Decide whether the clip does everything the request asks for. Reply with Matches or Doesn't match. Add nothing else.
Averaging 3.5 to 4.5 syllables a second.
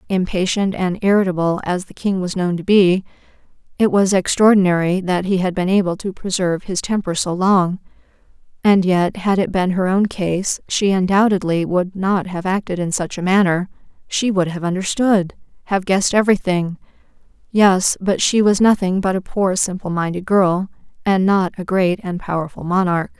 Doesn't match